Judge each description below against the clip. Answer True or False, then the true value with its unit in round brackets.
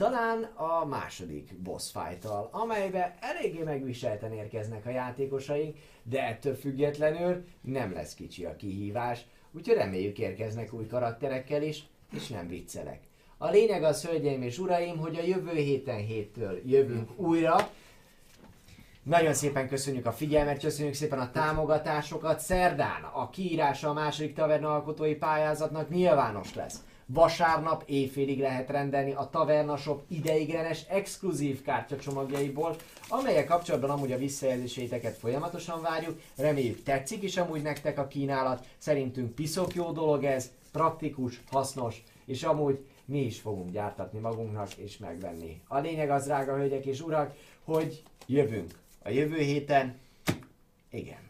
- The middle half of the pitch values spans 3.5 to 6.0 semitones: True (3.9 semitones)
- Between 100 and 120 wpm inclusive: False (130 wpm)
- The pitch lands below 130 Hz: False (140 Hz)